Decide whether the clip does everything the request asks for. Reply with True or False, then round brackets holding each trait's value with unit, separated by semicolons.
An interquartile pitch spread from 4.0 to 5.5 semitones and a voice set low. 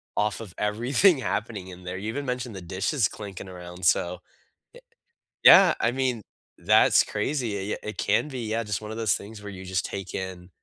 True (4.5 semitones; 105 Hz)